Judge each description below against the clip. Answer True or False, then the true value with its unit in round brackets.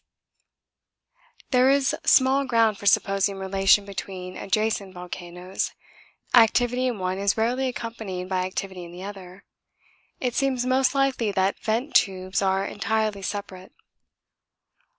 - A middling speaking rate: False (125 wpm)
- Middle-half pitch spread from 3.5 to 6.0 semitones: True (4.4 semitones)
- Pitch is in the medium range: False (200 Hz)